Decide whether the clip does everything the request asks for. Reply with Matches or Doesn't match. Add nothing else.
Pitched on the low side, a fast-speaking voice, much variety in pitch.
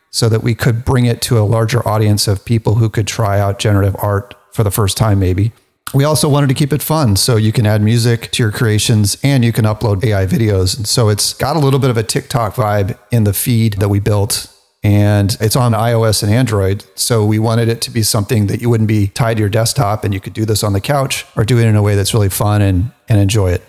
Doesn't match